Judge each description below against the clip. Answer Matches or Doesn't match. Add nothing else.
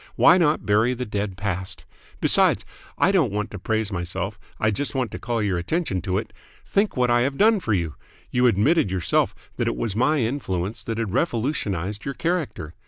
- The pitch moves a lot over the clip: Matches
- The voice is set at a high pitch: Doesn't match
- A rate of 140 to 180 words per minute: Doesn't match